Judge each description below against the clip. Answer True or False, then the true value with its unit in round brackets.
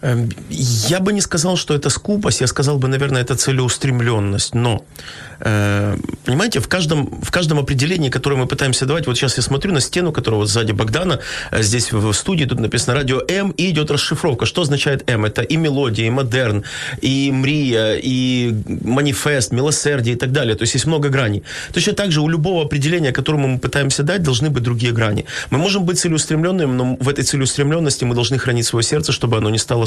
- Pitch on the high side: False (135 Hz)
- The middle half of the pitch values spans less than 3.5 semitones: False (3.8 semitones)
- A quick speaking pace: True (195 wpm)